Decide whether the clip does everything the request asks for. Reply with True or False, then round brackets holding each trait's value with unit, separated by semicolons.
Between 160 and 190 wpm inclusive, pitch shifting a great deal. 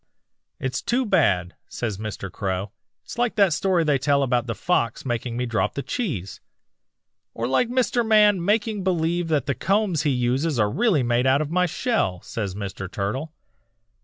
True (175 wpm; 8.7 semitones)